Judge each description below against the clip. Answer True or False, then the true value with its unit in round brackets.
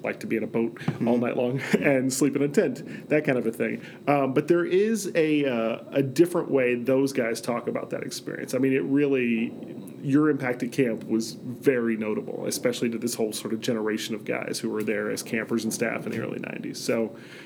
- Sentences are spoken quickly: True (225 wpm)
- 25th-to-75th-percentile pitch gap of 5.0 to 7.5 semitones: False (3.7 semitones)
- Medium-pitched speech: False (125 Hz)